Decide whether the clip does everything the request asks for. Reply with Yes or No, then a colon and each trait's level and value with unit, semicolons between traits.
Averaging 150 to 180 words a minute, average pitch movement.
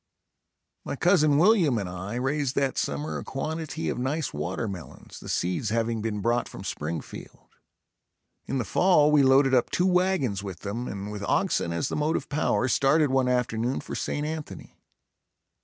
No: average, 165 wpm; wide, 6.4 semitones